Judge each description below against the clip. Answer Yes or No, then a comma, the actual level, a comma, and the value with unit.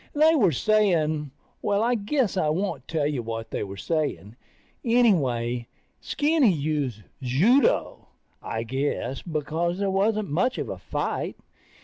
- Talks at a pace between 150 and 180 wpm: No, slow, 135 wpm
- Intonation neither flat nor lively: No, wide, 8.2 semitones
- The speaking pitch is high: No, medium, 165 Hz